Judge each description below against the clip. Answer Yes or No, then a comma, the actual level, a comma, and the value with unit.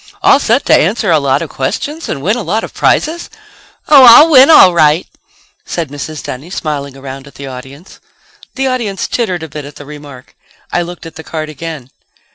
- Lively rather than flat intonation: Yes, wide, 7.5 semitones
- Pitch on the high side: No, medium, 160 Hz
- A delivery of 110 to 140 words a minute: No, average, 200 wpm